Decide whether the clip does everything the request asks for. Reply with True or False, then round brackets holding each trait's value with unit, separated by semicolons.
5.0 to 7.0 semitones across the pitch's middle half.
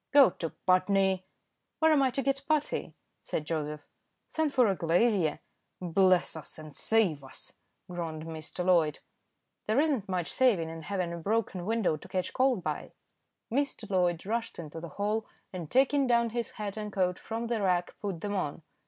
True (5.6 semitones)